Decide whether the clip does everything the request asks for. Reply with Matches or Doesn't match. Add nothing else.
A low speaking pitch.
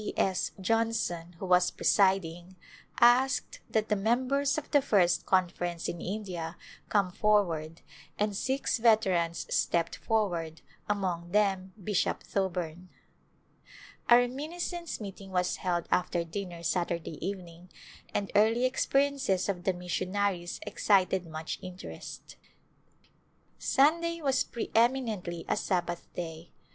Doesn't match